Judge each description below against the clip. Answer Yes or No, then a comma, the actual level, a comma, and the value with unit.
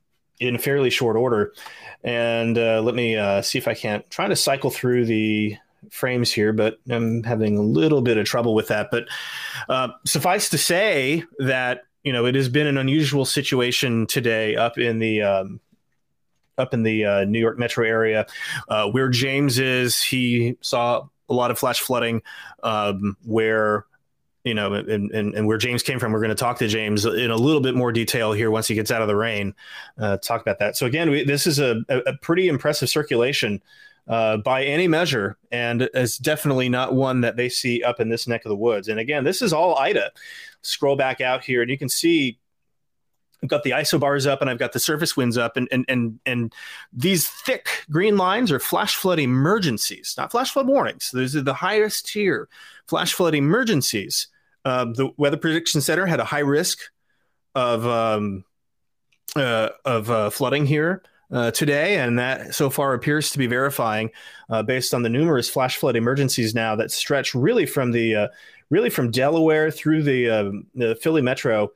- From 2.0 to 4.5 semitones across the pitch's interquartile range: Yes, average, 4.2 semitones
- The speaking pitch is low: Yes, low, 125 Hz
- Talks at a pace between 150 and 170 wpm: No, average, 195 wpm